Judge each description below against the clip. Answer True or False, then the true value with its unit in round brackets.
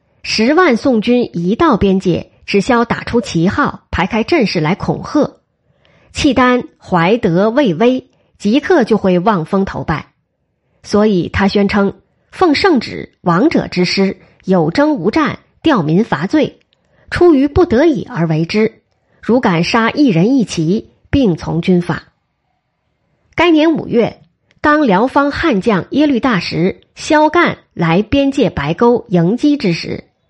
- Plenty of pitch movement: True (7.7 semitones)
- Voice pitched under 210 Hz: False (220 Hz)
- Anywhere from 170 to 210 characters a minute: True (195 characters per minute)